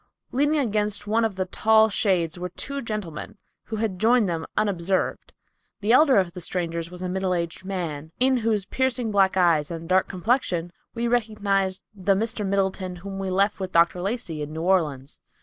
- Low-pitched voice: No, high, 190 Hz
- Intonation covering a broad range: No, average, 3.7 semitones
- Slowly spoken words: No, average, 185 wpm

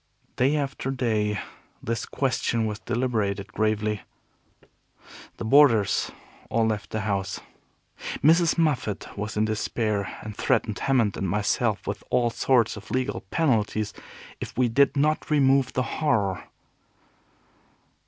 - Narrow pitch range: No, average, 4.1 semitones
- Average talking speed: No, slow, 125 wpm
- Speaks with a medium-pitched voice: No, low, 115 Hz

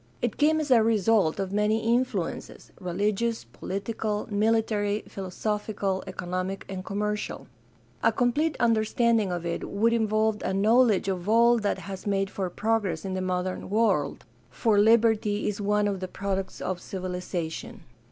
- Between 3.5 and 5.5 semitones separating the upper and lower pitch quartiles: No, average, 2.9 semitones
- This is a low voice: No, high, 205 Hz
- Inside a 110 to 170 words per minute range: Yes, average, 150 wpm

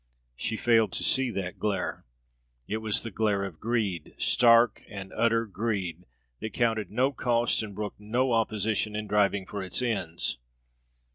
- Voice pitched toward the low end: Yes, low, 110 Hz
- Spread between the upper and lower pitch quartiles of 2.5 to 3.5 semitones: Yes, average, 2.8 semitones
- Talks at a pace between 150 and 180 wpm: Yes, average, 155 wpm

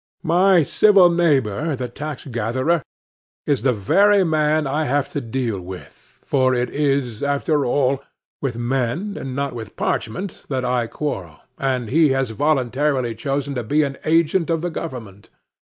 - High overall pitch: No, low, 135 Hz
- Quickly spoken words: No, average, 150 wpm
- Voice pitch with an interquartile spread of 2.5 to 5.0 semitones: Yes, average, 4.1 semitones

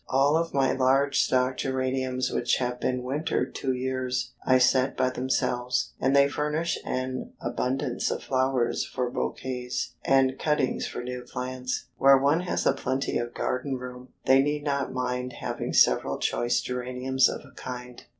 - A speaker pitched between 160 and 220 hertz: No, low, 130 Hz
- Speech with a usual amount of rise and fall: No, narrow, 1.3 semitones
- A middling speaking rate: Yes, average, 160 wpm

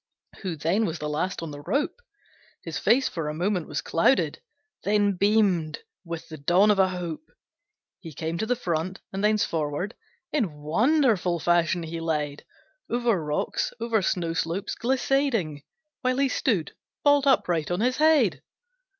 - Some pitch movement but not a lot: No, wide, 6.0 semitones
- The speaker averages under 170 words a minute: Yes, average, 160 wpm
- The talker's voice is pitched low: No, medium, 180 Hz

